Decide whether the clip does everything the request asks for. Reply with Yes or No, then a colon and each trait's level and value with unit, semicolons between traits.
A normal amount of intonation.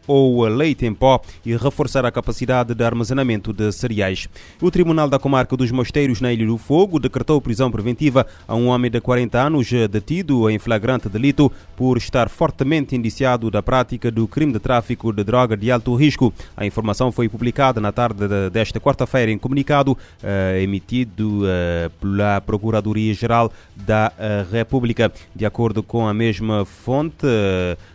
Yes: average, 3.3 semitones